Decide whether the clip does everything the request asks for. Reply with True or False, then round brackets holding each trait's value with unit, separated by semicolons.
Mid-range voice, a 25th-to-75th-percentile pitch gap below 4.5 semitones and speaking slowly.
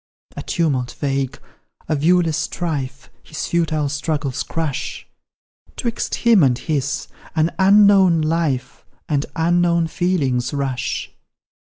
True (155 Hz; 3.8 semitones; 110 wpm)